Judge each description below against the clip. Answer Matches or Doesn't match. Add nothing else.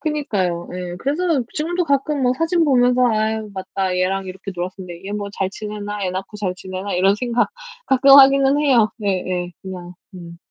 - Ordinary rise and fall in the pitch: Doesn't match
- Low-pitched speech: Doesn't match